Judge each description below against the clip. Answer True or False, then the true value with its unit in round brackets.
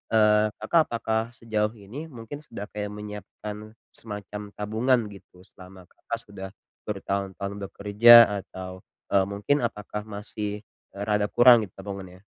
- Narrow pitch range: True (1.7 semitones)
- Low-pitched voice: True (105 Hz)